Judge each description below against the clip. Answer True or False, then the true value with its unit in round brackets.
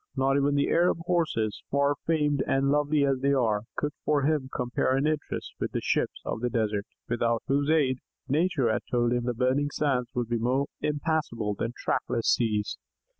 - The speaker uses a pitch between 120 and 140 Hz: True (135 Hz)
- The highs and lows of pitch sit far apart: False (3.5 semitones)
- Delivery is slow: False (185 wpm)